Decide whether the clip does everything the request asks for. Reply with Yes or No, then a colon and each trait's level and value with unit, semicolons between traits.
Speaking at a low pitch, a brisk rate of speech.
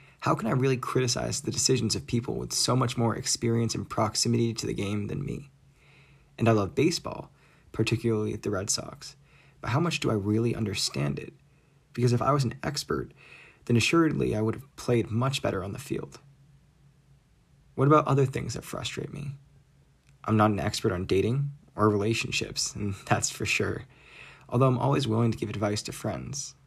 No: low, 125 Hz; average, 185 wpm